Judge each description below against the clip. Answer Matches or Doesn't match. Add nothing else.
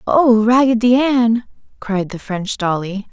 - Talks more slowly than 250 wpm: Matches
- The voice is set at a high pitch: Matches